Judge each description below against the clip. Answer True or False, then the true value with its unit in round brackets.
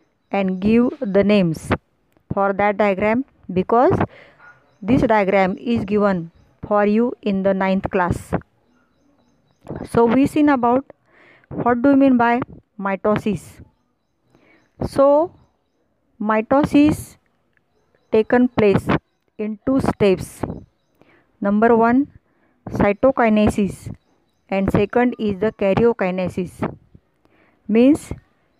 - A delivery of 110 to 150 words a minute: False (90 wpm)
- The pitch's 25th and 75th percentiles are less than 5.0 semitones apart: True (3.7 semitones)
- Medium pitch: False (215 Hz)